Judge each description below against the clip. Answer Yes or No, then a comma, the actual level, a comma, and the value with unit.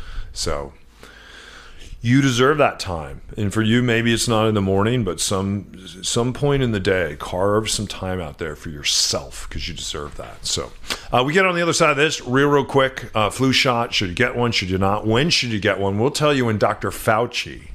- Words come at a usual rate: No, fast, 225 wpm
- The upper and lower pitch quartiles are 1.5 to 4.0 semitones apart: No, average, 4.4 semitones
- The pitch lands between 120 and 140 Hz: No, low, 110 Hz